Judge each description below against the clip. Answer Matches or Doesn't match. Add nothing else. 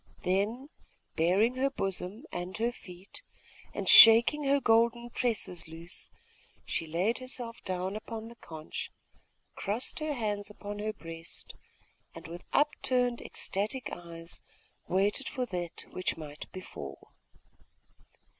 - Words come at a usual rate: Doesn't match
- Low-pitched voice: Doesn't match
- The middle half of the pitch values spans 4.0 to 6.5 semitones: Matches